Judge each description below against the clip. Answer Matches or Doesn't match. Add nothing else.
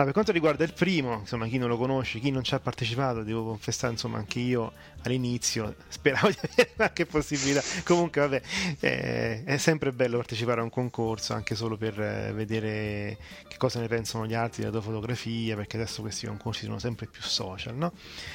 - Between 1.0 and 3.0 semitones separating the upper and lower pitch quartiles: Doesn't match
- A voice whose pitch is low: Matches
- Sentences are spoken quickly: Matches